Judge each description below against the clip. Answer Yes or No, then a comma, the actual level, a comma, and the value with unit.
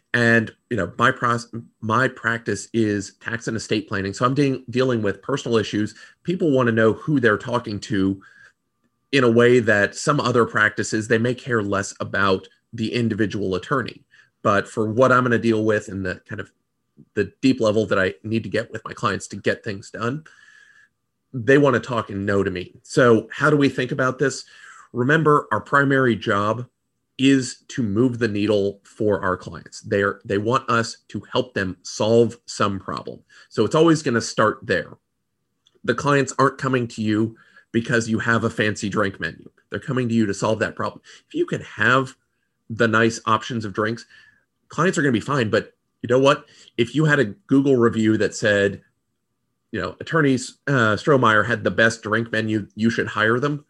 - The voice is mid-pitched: No, low, 115 Hz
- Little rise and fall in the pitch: No, average, 3.3 semitones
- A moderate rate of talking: Yes, average, 195 wpm